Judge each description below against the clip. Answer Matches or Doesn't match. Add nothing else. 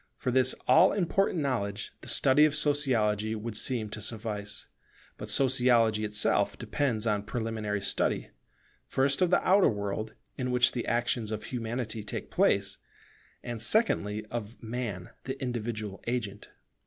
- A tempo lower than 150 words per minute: Matches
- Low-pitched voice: Matches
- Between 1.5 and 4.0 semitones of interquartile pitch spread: Matches